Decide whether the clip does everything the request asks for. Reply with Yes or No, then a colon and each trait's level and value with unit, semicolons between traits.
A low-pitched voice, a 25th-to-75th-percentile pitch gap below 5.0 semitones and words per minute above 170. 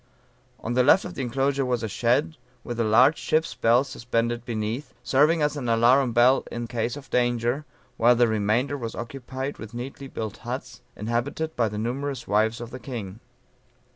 Yes: low, 120 Hz; average, 2.9 semitones; average, 180 wpm